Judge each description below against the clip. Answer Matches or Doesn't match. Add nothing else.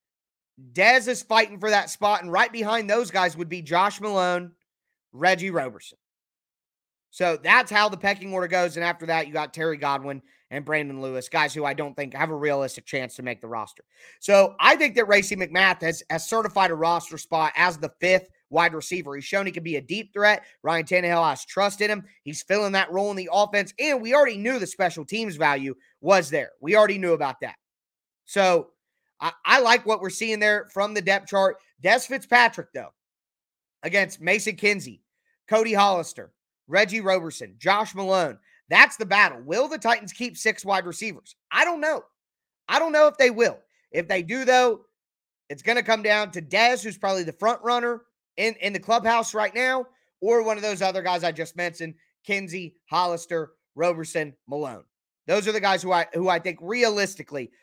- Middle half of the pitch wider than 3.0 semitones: Matches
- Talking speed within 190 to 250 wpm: Matches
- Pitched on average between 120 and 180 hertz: Doesn't match